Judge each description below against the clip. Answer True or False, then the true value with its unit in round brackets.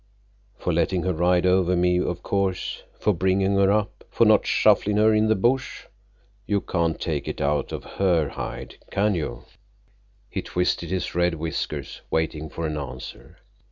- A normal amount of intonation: True (3.2 semitones)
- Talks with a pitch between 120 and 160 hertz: False (90 Hz)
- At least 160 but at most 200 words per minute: True (165 wpm)